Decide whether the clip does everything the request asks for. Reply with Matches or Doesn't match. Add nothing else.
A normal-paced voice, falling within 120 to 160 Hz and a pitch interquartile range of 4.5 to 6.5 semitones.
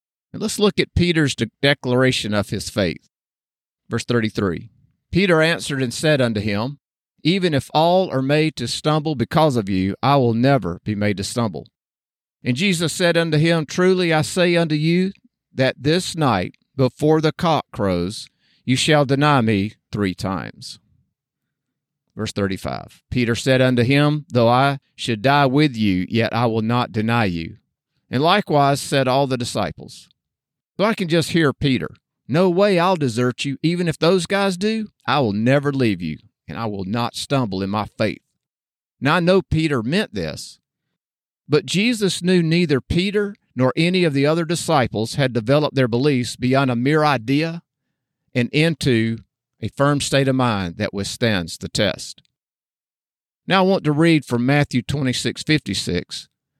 Matches